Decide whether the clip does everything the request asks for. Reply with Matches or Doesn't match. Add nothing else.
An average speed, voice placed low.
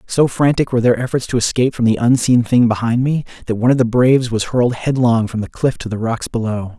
Doesn't match